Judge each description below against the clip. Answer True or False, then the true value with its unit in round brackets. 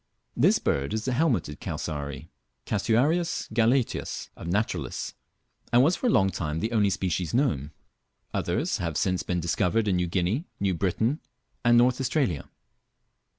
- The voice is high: False (100 Hz)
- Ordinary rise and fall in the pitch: False (6.2 semitones)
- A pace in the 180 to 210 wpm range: False (150 wpm)